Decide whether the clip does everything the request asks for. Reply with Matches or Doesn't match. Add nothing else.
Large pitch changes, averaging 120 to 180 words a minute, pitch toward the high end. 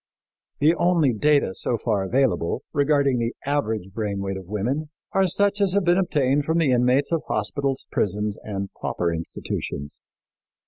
Doesn't match